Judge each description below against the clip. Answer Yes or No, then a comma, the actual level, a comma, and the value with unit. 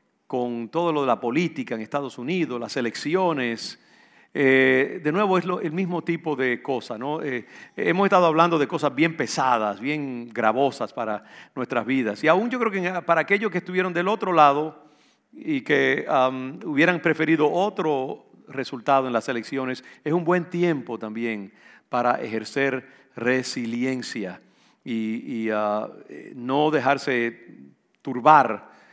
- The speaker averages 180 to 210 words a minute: No, average, 145 wpm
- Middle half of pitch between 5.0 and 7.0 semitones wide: Yes, wide, 5.6 semitones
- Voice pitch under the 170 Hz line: Yes, medium, 140 Hz